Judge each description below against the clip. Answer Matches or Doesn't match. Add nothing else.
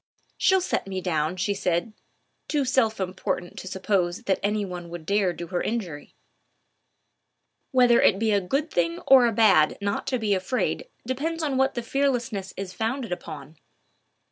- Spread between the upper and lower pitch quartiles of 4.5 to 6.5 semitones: Matches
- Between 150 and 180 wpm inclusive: Matches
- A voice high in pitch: Matches